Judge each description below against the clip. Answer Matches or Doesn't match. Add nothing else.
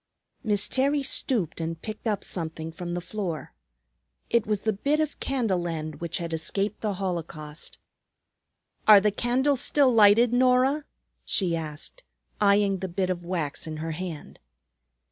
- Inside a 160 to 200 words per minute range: Doesn't match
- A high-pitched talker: Matches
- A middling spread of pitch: Doesn't match